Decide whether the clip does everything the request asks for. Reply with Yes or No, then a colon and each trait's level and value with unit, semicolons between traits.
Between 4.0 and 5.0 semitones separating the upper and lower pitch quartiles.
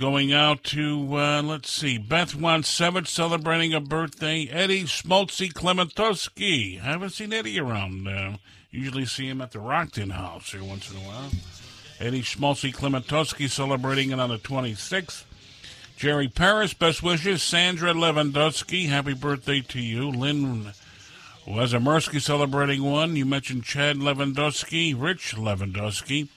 Yes: average, 4.4 semitones